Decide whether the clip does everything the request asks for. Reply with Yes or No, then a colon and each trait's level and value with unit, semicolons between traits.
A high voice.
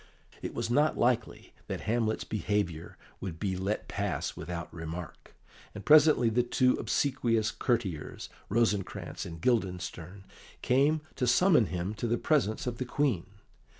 No: low, 110 Hz